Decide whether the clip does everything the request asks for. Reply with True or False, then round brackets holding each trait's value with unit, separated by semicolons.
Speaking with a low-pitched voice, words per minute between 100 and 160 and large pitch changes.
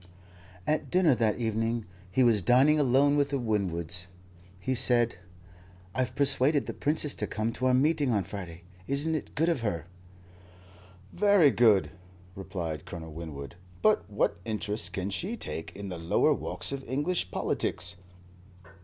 True (115 Hz; 150 wpm; 7.2 semitones)